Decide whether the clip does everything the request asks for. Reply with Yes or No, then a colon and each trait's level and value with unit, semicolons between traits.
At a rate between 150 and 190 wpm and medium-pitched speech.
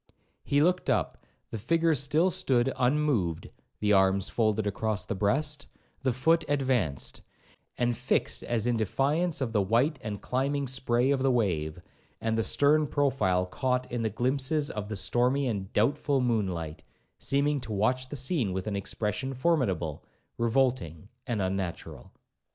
No: average, 155 wpm; low, 120 Hz